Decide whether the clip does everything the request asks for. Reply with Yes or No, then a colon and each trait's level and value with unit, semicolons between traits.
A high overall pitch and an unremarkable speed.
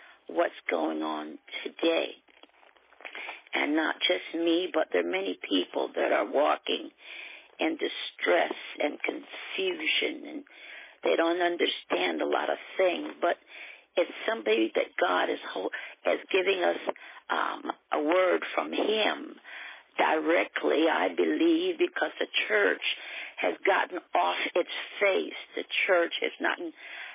No: very high, 315 Hz; slow, 130 wpm